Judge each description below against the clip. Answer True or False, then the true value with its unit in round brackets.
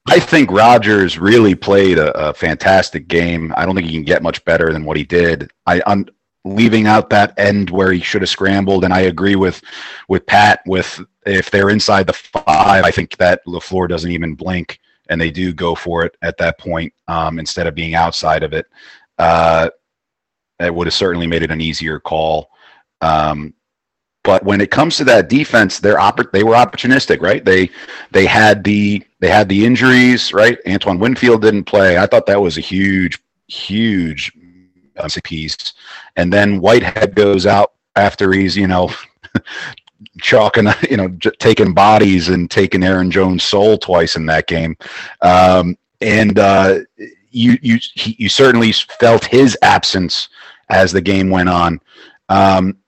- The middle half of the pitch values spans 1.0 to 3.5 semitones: True (3.1 semitones)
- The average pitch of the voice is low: True (95 Hz)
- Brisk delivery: False (170 wpm)